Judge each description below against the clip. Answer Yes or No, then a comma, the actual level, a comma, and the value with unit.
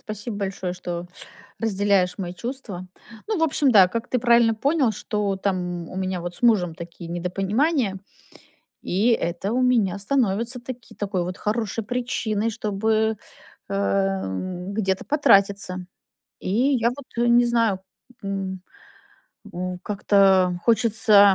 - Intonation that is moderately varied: Yes, average, 3.9 semitones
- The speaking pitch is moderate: No, high, 200 Hz